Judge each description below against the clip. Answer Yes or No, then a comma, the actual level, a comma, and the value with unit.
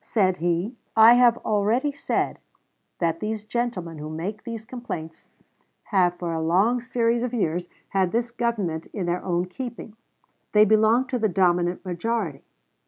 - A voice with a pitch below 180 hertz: No, high, 210 Hz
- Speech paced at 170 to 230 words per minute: No, average, 155 wpm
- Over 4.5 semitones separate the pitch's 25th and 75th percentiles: Yes, average, 5.1 semitones